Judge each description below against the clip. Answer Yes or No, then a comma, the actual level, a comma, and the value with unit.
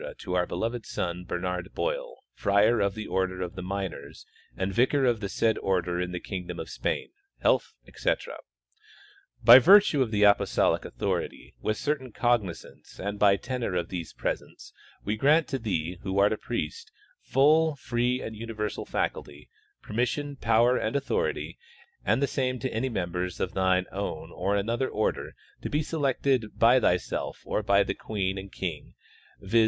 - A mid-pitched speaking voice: No, low, 105 Hz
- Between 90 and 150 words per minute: No, average, 160 wpm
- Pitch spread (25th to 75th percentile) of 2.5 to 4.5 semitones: No, average, 5.3 semitones